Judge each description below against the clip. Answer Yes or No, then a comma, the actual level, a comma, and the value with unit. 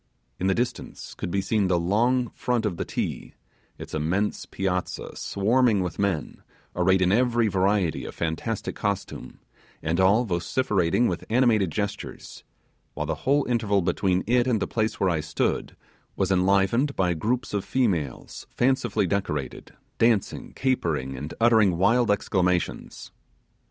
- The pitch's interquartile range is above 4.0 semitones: Yes, average, 4.5 semitones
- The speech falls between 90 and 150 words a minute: Yes, average, 145 wpm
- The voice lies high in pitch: No, low, 100 Hz